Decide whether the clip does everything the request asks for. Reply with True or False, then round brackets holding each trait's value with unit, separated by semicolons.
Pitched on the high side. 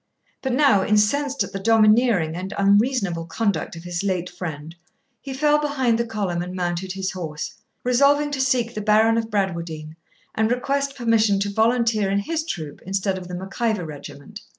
True (210 Hz)